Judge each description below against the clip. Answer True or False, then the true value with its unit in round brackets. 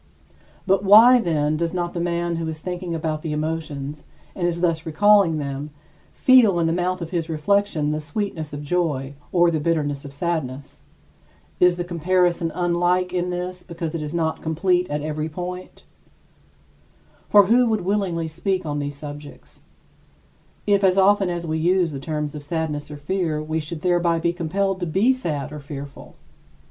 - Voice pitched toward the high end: False (170 Hz)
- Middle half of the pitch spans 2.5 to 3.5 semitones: True (3.0 semitones)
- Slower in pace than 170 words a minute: False (175 wpm)